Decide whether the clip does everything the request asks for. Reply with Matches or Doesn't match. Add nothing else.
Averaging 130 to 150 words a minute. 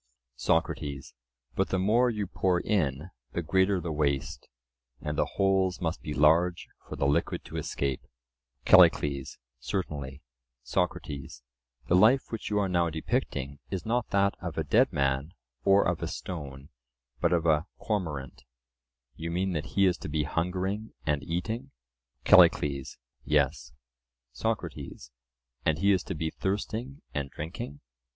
Matches